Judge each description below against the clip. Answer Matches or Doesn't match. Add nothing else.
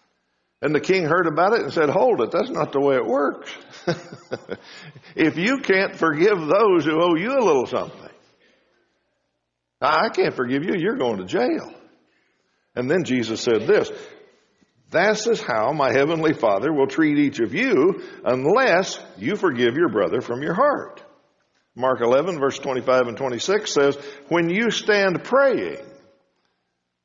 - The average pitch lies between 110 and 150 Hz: Doesn't match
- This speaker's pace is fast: Doesn't match